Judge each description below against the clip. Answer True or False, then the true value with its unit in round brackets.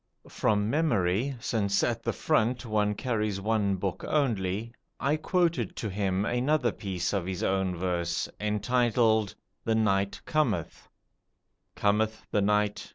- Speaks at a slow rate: True (130 wpm)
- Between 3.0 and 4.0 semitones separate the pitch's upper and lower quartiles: True (3.6 semitones)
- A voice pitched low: True (105 Hz)